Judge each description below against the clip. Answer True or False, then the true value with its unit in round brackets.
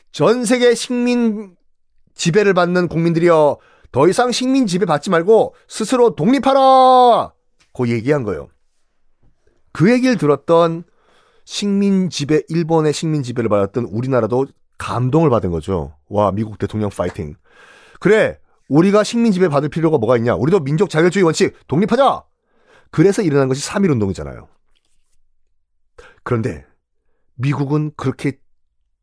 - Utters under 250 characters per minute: False (285 characters per minute)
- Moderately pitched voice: True (160 Hz)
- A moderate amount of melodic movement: False (8.9 semitones)